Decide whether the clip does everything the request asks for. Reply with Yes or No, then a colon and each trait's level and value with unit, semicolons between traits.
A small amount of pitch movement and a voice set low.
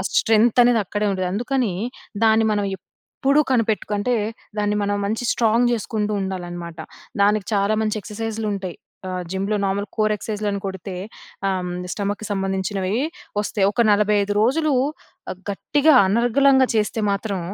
No: narrow, 2.3 semitones; high, 210 Hz